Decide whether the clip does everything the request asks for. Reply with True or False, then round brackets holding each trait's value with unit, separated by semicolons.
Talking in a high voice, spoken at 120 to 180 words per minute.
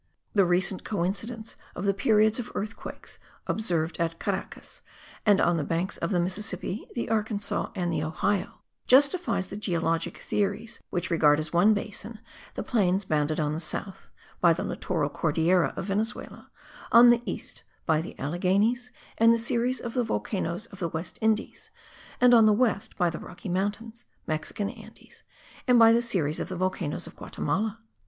True (195 Hz; 170 wpm)